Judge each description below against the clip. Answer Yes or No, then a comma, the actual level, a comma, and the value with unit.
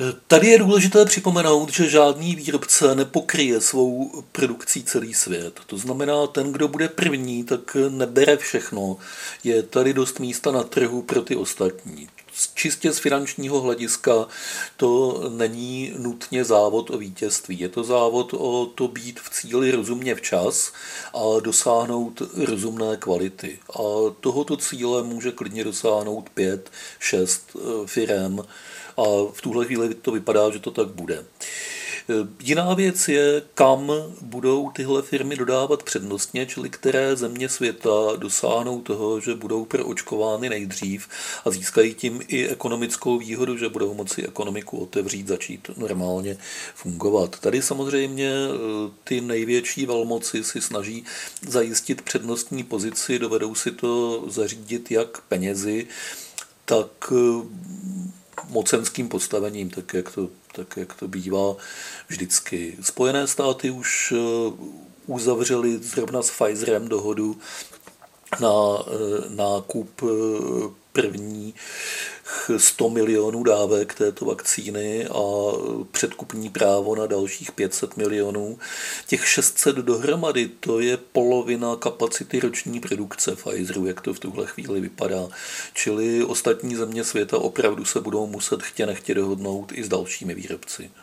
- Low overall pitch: Yes, low, 120 Hz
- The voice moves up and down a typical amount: Yes, average, 3.8 semitones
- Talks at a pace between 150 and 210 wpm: No, average, 125 wpm